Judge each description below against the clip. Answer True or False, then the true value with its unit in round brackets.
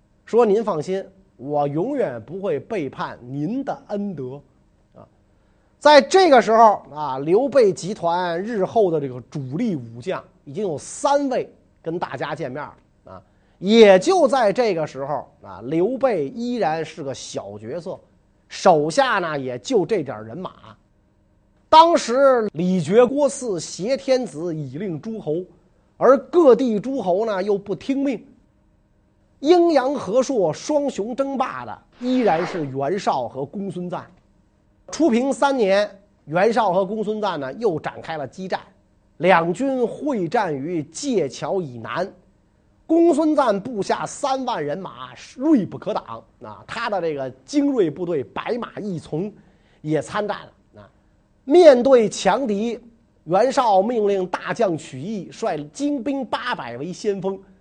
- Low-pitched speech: False (195 Hz)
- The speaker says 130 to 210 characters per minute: True (200 characters per minute)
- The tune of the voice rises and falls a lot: True (9.0 semitones)